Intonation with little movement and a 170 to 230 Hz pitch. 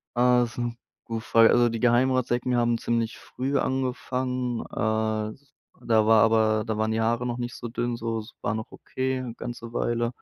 No: narrow, 1.8 semitones; low, 120 Hz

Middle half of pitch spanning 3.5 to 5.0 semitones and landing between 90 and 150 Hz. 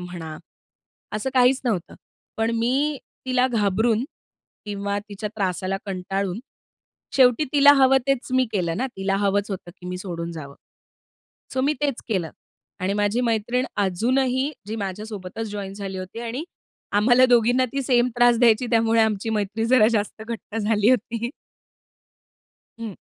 No: average, 4.0 semitones; high, 220 Hz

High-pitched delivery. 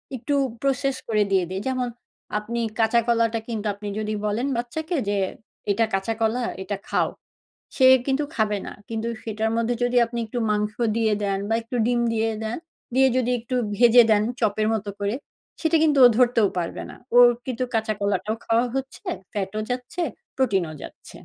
Yes: high, 225 Hz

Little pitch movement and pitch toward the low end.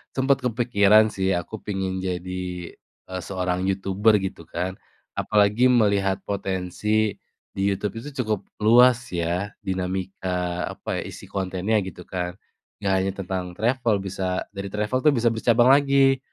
No: average, 3.1 semitones; low, 100 Hz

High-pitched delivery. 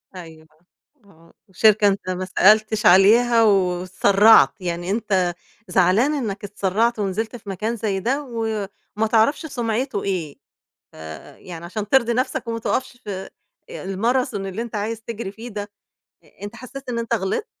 Yes: high, 210 Hz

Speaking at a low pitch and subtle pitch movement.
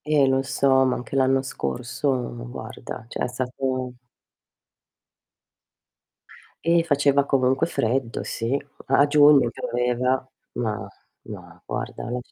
Yes: low, 130 Hz; narrow, 2.1 semitones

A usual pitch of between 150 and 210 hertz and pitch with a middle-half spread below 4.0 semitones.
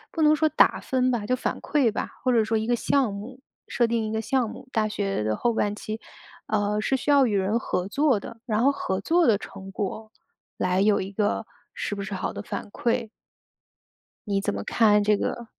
No: high, 220 Hz; average, 3.4 semitones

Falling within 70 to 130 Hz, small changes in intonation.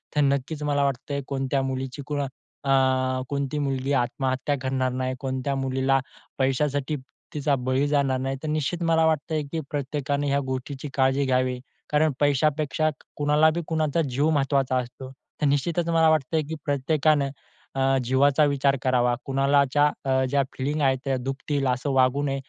No: medium, 140 Hz; narrow, 1.9 semitones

